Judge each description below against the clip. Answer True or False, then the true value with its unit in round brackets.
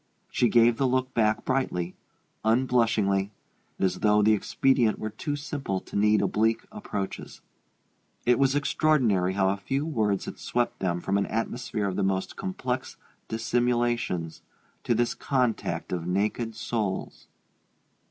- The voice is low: True (115 Hz)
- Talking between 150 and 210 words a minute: False (140 wpm)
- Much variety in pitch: False (4.1 semitones)